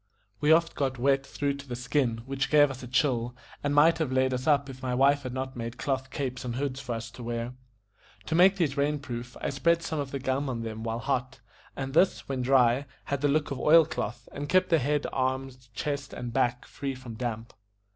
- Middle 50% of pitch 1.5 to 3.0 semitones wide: Yes, narrow, 2.5 semitones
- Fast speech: Yes, fast, 230 wpm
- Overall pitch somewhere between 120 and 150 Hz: Yes, low, 135 Hz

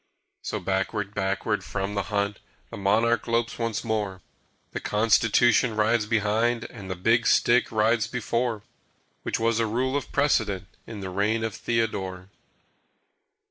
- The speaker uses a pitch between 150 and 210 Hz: No, low, 110 Hz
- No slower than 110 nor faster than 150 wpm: Yes, average, 140 wpm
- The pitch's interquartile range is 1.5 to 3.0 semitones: Yes, narrow, 2.6 semitones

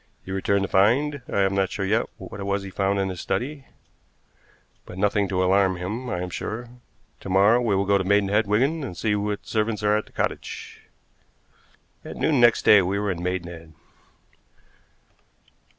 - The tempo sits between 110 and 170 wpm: No, average, 185 wpm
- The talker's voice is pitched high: No, low, 100 Hz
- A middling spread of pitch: No, narrow, 2.3 semitones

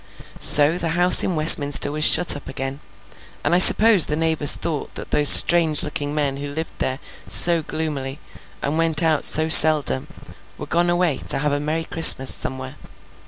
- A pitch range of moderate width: No, narrow, 2.3 semitones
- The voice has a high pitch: No, medium, 155 Hz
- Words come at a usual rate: Yes, average, 175 wpm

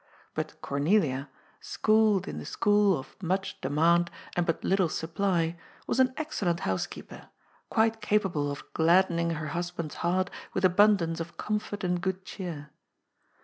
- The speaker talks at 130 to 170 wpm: Yes, average, 140 wpm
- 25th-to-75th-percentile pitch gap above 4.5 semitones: No, average, 3.5 semitones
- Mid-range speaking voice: Yes, medium, 175 Hz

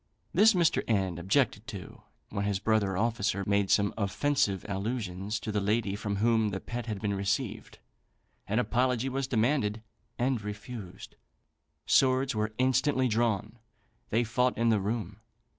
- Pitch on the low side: Yes, low, 110 Hz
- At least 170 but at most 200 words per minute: No, average, 145 wpm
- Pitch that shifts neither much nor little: Yes, average, 3.5 semitones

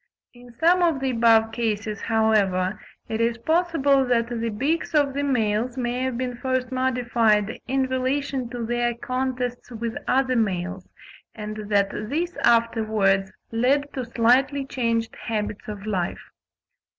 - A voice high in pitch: Yes, high, 240 Hz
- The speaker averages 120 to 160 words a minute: Yes, average, 140 wpm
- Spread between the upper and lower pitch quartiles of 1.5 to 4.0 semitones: Yes, average, 3.0 semitones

